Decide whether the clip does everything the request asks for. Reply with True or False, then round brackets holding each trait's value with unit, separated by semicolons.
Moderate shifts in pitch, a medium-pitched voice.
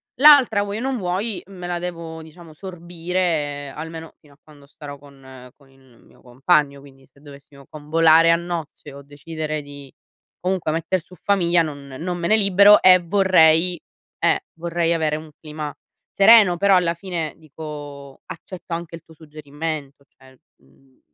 True (3.7 semitones; 160 Hz)